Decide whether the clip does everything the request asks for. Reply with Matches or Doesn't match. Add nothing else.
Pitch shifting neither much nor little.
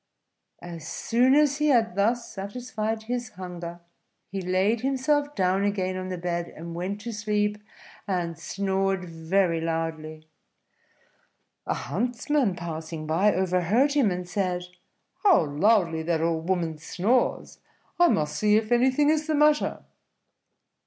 Doesn't match